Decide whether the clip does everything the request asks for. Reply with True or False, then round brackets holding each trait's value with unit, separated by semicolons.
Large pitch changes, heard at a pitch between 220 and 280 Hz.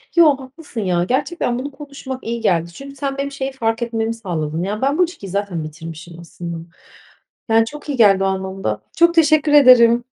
True (6.7 semitones; 235 Hz)